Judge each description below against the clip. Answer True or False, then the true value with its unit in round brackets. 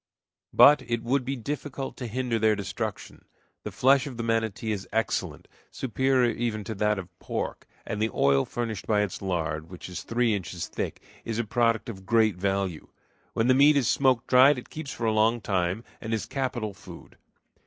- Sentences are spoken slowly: False (190 wpm)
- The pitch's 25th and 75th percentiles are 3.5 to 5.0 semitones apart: True (3.9 semitones)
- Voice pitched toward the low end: True (115 Hz)